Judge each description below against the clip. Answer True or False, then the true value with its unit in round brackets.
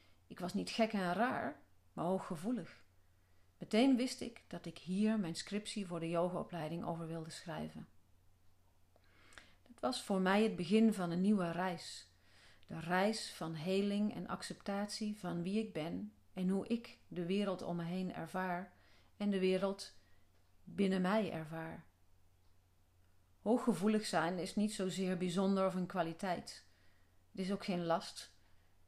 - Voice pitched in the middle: True (175 Hz)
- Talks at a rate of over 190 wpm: False (150 wpm)